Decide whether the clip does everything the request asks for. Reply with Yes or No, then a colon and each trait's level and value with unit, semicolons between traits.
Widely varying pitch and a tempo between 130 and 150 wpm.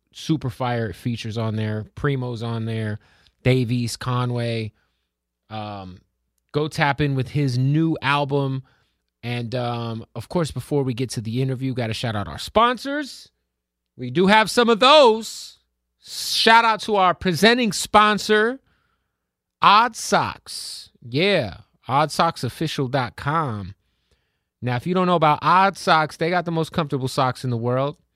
Yes: wide, 6.7 semitones; average, 145 wpm